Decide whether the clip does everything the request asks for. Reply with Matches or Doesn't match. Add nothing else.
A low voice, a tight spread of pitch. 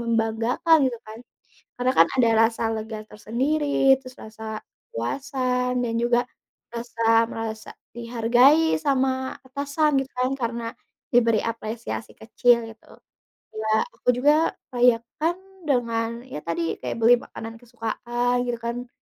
Doesn't match